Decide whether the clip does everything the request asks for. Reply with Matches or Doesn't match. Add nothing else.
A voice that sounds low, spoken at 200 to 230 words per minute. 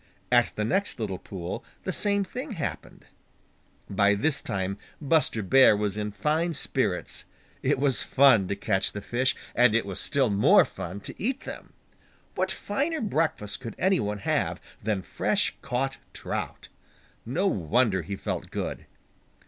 Doesn't match